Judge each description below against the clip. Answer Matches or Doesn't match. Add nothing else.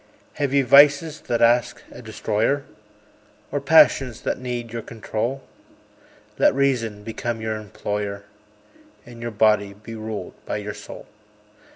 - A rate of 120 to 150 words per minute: Matches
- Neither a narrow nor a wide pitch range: Matches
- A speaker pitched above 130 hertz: Doesn't match